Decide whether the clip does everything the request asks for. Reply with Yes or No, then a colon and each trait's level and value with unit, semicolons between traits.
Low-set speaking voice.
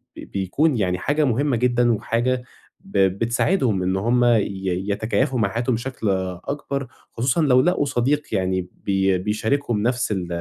Yes: low, 120 Hz